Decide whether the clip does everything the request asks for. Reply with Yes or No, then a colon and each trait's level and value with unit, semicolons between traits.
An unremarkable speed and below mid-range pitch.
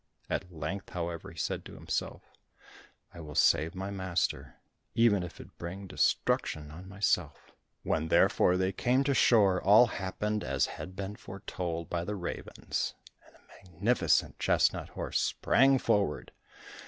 Yes: average, 145 wpm; very low, 95 Hz